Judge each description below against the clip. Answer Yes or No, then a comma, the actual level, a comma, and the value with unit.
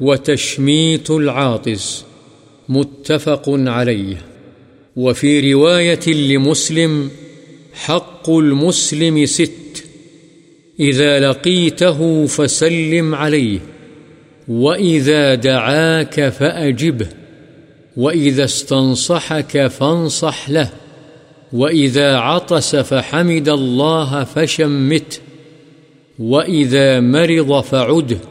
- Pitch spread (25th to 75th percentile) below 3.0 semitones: Yes, narrow, 2.4 semitones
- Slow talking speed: Yes, slow, 60 wpm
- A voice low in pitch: No, medium, 150 Hz